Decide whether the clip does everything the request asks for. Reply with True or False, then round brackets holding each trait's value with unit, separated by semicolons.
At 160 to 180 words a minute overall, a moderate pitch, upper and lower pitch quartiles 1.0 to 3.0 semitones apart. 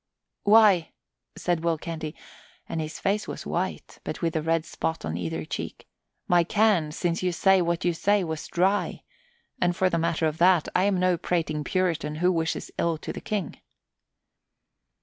True (175 wpm; 170 Hz; 2.5 semitones)